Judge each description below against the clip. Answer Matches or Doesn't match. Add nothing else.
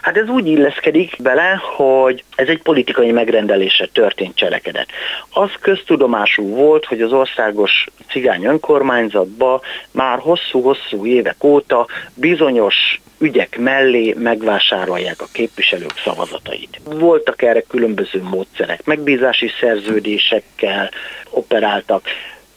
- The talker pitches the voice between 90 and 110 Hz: Doesn't match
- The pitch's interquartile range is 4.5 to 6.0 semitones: Matches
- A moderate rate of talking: Doesn't match